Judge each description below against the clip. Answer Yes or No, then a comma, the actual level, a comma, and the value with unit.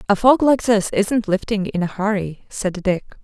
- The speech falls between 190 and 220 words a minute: Yes, fast, 205 wpm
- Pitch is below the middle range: No, high, 205 Hz